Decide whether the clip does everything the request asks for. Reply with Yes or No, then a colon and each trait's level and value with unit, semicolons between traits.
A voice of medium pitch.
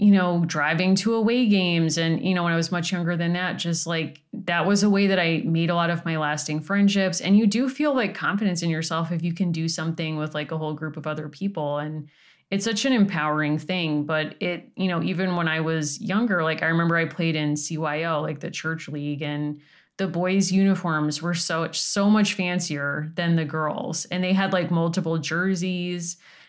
Yes: medium, 170 Hz